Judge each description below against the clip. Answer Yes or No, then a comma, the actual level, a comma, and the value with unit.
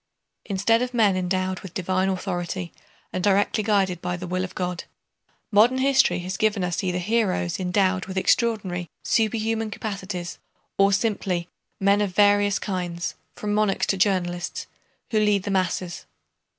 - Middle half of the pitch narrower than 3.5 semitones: Yes, narrow, 2.4 semitones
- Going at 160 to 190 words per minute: No, average, 150 wpm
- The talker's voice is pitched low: No, high, 190 Hz